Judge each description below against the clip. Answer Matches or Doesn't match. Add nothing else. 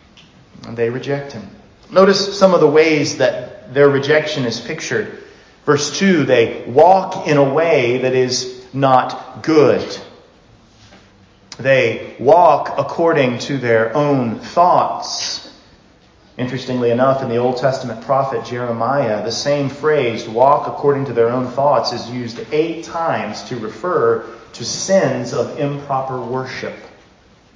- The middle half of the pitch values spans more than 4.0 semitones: Doesn't match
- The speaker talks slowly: Matches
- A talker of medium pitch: Doesn't match